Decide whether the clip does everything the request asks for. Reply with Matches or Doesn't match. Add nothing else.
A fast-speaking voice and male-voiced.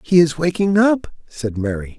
Doesn't match